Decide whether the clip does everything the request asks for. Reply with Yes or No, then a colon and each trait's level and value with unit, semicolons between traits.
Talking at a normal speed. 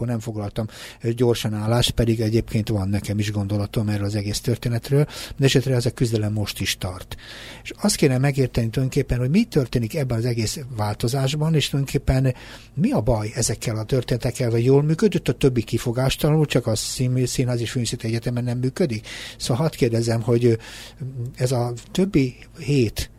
No: fast, 165 wpm